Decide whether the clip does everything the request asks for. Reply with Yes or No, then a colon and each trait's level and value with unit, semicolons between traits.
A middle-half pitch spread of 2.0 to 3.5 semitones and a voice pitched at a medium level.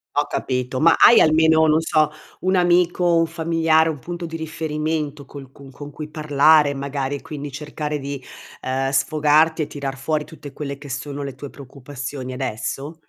Yes: narrow, 2.5 semitones; medium, 150 Hz